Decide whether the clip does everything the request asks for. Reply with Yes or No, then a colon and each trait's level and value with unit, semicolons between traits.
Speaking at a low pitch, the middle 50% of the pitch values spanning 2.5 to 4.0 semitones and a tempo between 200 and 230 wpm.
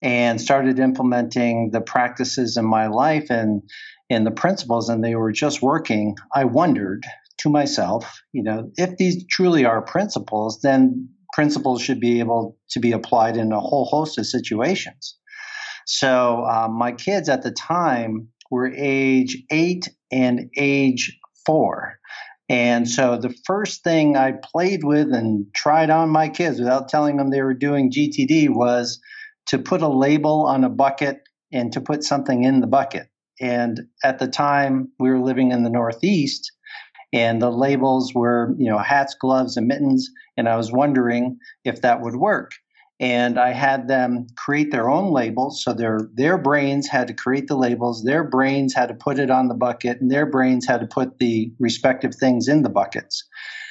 No: low, 130 Hz; average, 3.5 semitones; average, 175 wpm